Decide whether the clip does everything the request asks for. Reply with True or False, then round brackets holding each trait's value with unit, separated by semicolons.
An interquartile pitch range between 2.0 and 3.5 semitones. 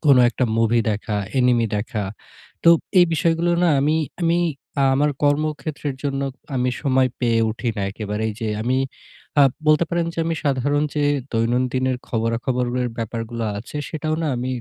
False (4.4 semitones)